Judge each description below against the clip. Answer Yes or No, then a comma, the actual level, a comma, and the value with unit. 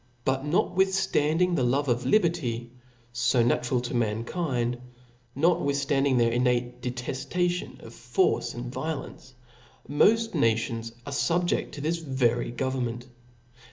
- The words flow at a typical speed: No, slow, 125 wpm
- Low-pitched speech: Yes, low, 130 Hz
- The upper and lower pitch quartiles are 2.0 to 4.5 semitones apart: No, average, 5.0 semitones